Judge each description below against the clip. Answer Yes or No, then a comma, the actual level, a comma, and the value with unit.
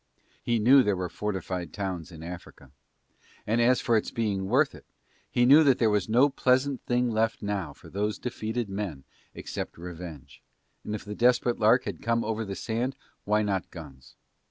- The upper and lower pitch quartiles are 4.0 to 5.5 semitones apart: Yes, average, 4.4 semitones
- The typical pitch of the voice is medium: No, low, 105 Hz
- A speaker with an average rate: Yes, average, 180 wpm